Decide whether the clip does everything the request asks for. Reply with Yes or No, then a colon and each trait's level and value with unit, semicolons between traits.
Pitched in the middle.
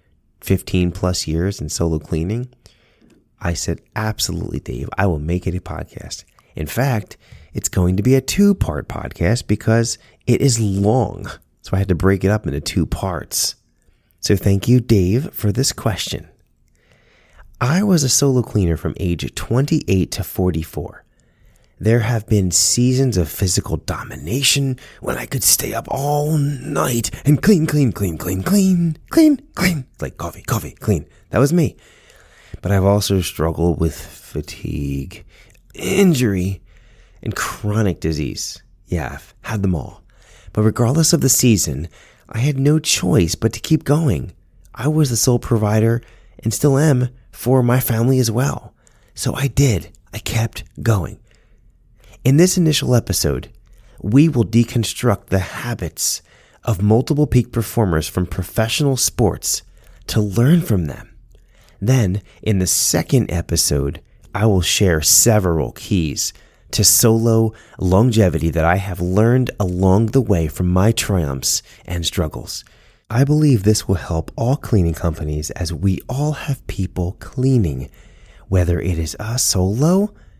No: low, 105 Hz